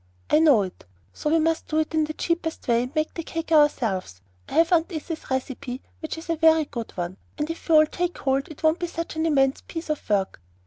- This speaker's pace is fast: Yes, fast, 240 wpm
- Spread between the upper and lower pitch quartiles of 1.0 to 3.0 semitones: No, average, 3.6 semitones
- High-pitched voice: Yes, very high, 310 Hz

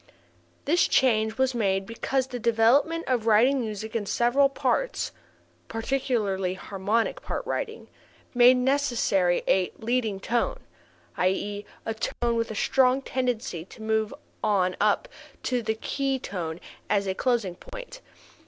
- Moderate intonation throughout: Yes, average, 4.1 semitones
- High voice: Yes, high, 230 Hz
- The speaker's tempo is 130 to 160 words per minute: Yes, slow, 135 wpm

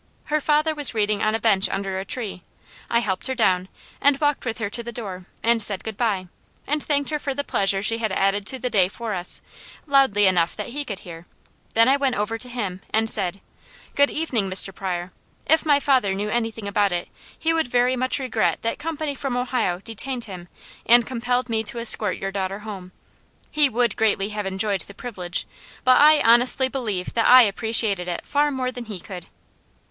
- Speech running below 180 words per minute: No, fast, 205 wpm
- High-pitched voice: Yes, high, 225 Hz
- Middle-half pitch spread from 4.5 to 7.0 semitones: Yes, average, 4.8 semitones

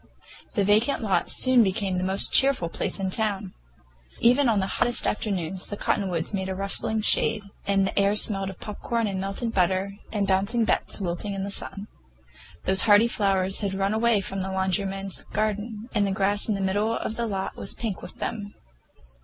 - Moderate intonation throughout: No, narrow, 2.1 semitones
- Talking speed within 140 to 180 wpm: No, average, 190 wpm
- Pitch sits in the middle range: No, high, 200 Hz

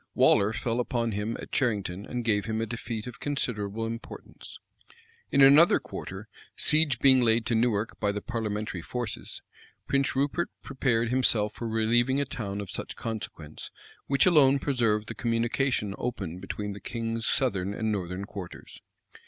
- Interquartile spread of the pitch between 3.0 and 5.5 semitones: Yes, average, 3.3 semitones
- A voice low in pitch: Yes, low, 115 Hz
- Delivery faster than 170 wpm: No, average, 155 wpm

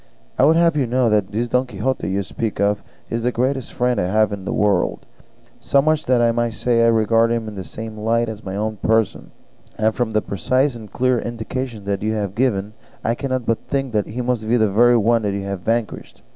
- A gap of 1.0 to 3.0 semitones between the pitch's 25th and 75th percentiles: Yes, narrow, 2.6 semitones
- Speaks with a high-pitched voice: No, low, 115 Hz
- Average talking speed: No, fast, 230 wpm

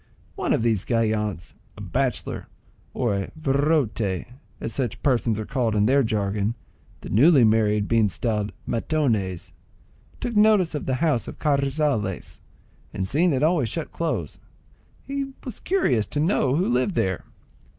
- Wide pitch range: Yes, wide, 6.1 semitones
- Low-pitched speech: Yes, low, 125 Hz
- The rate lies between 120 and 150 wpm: Yes, average, 140 wpm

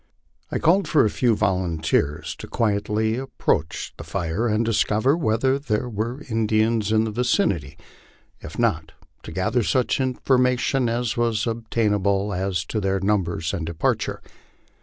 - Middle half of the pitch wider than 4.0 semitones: No, average, 3.7 semitones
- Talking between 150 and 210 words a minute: No, average, 140 wpm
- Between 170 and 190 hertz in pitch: No, low, 110 Hz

